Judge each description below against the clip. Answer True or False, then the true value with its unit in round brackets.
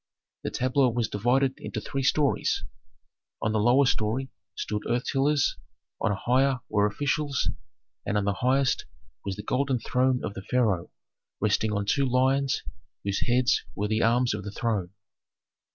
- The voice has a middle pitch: False (125 Hz)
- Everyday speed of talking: True (160 wpm)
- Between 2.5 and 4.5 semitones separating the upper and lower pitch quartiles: True (4.1 semitones)